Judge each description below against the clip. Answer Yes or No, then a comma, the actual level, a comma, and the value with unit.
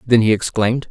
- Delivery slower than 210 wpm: Yes, average, 200 wpm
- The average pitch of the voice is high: No, low, 115 Hz